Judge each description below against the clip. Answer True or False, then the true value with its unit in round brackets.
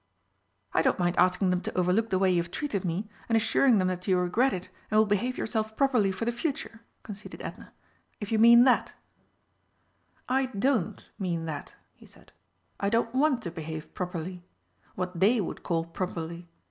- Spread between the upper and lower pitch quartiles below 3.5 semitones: False (4.4 semitones)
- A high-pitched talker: True (195 Hz)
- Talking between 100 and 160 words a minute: False (185 wpm)